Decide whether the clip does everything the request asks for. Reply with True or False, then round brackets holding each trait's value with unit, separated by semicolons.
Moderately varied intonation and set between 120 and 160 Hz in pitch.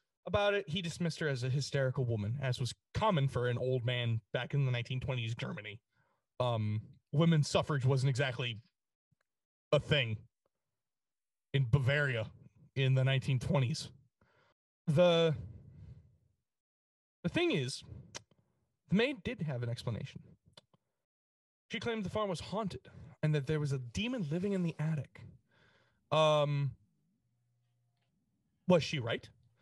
True (4.4 semitones; 135 Hz)